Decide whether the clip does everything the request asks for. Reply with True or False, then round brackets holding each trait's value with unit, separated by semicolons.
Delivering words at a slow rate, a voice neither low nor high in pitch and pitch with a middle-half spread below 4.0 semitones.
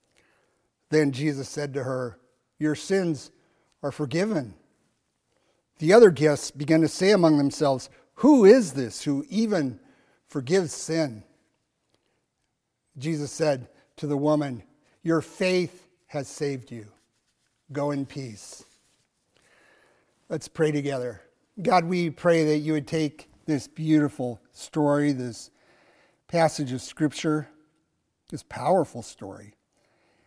True (115 wpm; 150 Hz; 2.9 semitones)